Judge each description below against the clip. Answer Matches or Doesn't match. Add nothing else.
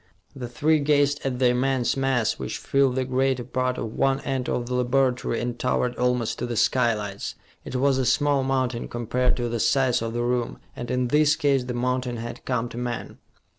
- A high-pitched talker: Doesn't match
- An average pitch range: Doesn't match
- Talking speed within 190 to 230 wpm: Matches